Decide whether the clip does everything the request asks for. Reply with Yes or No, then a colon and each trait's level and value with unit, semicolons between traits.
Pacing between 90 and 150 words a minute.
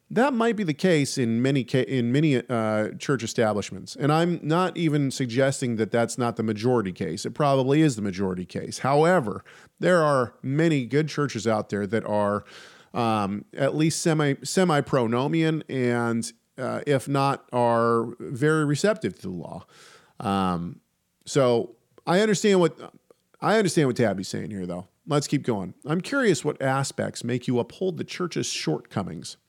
No: average, 160 wpm